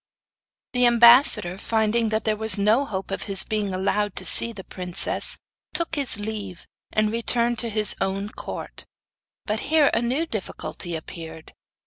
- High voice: Yes, high, 215 Hz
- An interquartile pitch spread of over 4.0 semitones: No, average, 3.4 semitones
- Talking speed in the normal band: Yes, average, 155 wpm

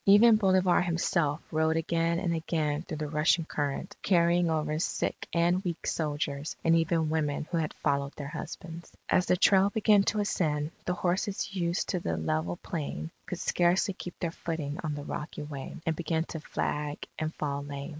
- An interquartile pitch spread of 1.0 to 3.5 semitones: Yes, average, 2.9 semitones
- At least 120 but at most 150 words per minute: No, average, 180 wpm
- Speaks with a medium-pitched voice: Yes, medium, 160 Hz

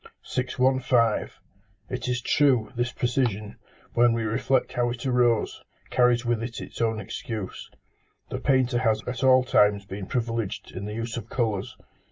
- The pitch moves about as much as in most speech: No, narrow, 2.2 semitones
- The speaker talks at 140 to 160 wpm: Yes, average, 155 wpm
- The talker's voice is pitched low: Yes, low, 120 Hz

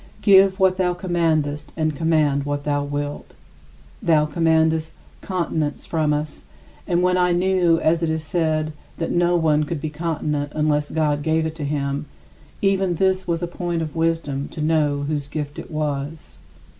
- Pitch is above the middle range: No, medium, 160 Hz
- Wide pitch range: No, narrow, 2.6 semitones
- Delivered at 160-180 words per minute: Yes, average, 170 wpm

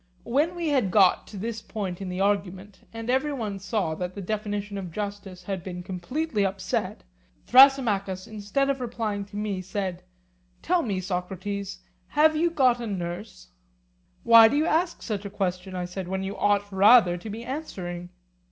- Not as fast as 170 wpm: No, average, 175 wpm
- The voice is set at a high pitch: Yes, high, 205 Hz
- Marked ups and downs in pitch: No, average, 3.8 semitones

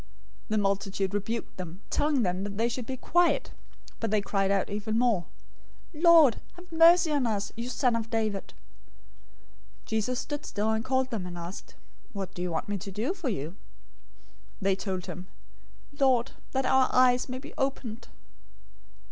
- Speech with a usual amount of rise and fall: Yes, average, 4.8 semitones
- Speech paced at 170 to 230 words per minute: Yes, average, 175 wpm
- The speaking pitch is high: Yes, high, 225 Hz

